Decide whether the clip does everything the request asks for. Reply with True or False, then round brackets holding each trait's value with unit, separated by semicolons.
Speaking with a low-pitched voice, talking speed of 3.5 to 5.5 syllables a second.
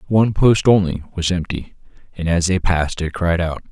True (90 Hz; 5.4 syllables/s)